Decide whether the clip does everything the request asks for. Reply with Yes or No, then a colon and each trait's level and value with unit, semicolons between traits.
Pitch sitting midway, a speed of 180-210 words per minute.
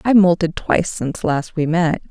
Yes: medium, 170 Hz; average, 200 wpm